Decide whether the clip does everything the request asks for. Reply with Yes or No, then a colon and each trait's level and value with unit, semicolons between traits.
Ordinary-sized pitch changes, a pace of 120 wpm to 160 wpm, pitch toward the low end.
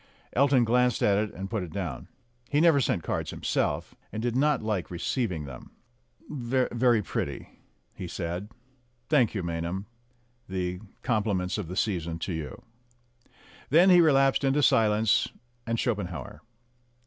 No: wide, 5.9 semitones; average, 145 wpm; low, 105 Hz